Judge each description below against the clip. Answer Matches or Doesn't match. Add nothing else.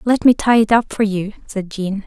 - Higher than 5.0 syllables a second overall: Doesn't match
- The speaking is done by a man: Doesn't match